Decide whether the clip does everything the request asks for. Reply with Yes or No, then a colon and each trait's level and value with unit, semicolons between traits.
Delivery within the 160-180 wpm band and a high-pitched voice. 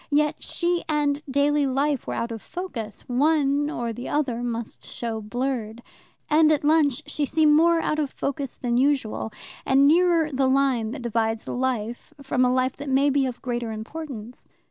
Yes: average, 175 wpm; very high, 270 Hz